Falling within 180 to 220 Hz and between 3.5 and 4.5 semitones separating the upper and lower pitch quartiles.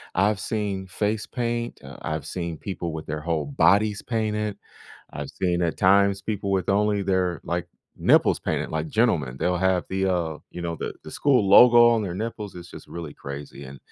No: very low, 95 Hz; average, 3.8 semitones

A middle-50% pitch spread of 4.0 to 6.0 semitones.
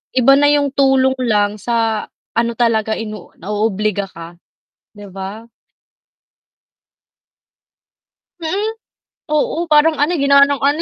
Yes: average, 5.2 semitones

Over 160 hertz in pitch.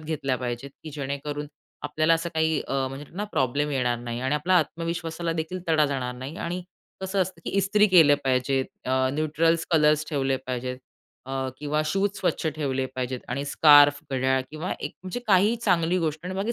No: medium, 150 Hz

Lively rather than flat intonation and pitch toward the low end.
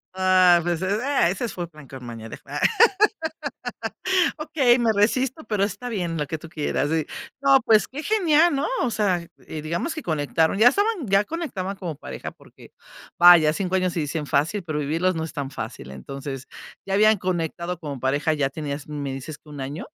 No: wide, 6.3 semitones; medium, 175 Hz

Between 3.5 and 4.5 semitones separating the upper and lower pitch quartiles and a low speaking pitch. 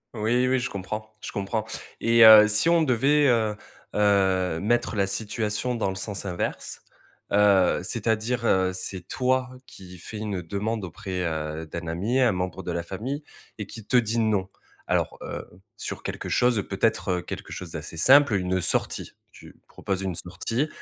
Yes: average, 4.0 semitones; low, 105 Hz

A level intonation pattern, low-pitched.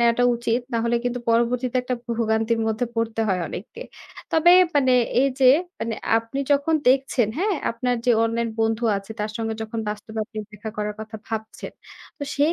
No: narrow, 2.2 semitones; high, 230 Hz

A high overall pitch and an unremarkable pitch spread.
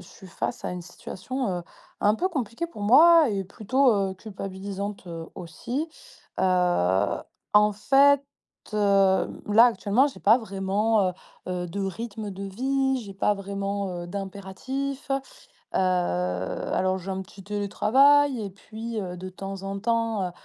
Yes: high, 200 Hz; average, 3.8 semitones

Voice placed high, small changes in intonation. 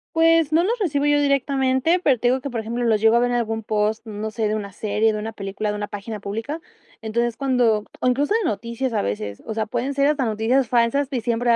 No: high, 235 Hz; average, 4.1 semitones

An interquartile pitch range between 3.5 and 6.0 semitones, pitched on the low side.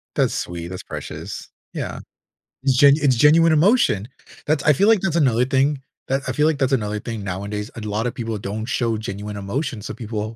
Yes: wide, 5.5 semitones; low, 120 Hz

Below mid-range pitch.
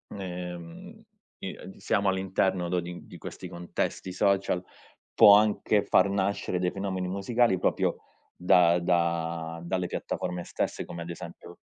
Yes: very low, 90 Hz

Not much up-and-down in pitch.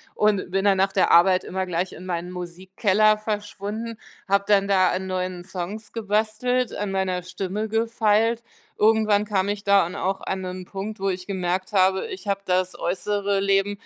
Yes: narrow, 2.2 semitones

